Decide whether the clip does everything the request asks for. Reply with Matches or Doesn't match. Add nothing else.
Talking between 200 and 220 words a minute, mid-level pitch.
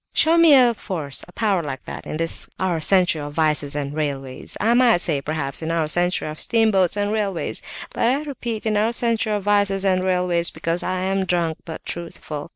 Matches